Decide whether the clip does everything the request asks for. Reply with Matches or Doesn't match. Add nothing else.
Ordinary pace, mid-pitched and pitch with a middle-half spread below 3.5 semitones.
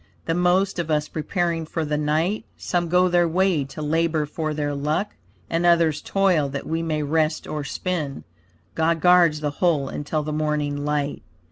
Matches